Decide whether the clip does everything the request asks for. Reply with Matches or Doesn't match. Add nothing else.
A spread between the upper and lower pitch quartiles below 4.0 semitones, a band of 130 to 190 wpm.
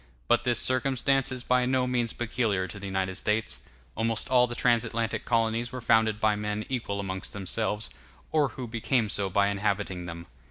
Matches